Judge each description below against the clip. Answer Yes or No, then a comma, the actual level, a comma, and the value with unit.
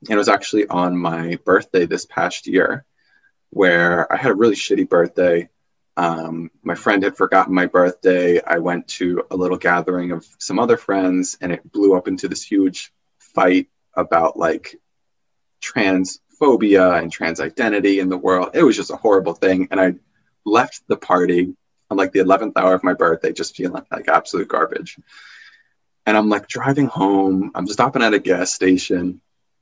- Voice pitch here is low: Yes, very low, 90 Hz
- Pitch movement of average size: No, narrow, 1.4 semitones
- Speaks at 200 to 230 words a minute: No, average, 175 wpm